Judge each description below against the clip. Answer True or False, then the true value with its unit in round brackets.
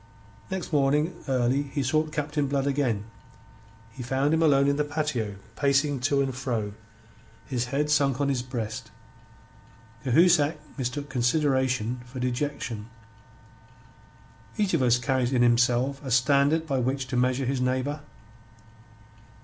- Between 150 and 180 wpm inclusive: False (135 wpm)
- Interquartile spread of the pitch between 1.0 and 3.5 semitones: True (2.6 semitones)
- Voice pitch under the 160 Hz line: True (135 Hz)